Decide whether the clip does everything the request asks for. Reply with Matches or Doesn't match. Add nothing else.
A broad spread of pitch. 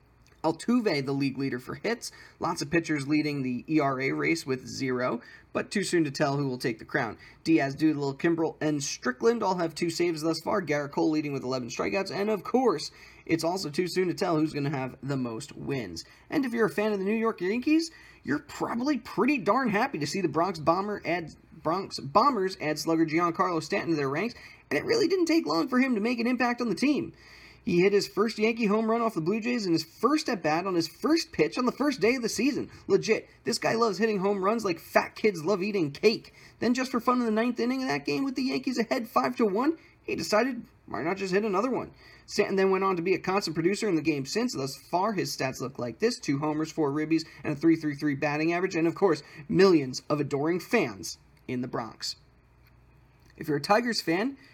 Matches